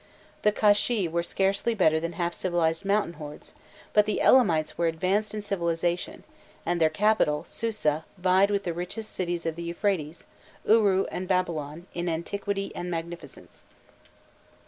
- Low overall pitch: No, medium, 175 Hz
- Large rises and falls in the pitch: No, average, 3.4 semitones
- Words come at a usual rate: Yes, average, 145 wpm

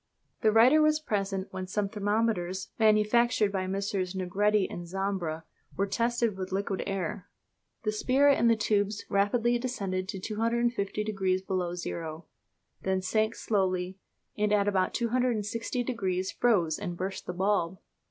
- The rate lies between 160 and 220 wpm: No, average, 145 wpm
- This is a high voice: Yes, high, 200 Hz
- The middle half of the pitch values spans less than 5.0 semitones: Yes, average, 3.1 semitones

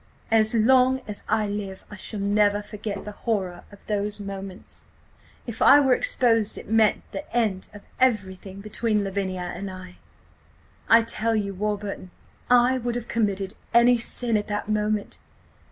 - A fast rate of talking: No, average, 155 wpm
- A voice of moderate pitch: No, high, 210 Hz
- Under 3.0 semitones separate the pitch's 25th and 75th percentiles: Yes, narrow, 2.5 semitones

